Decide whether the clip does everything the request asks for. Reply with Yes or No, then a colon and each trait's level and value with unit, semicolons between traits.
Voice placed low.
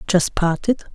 No: medium, 185 Hz